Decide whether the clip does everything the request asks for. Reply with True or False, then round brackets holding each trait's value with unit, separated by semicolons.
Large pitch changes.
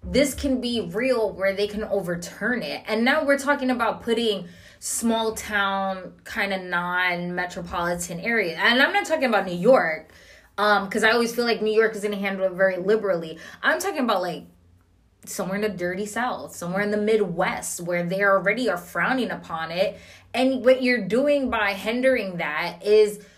False (4.0 semitones)